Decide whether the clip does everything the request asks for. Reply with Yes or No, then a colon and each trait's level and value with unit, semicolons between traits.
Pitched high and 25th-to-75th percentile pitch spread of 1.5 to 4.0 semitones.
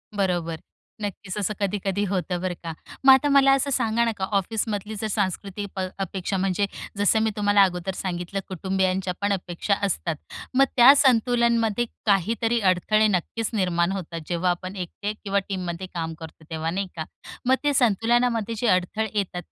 Yes: high, 200 Hz; average, 3.4 semitones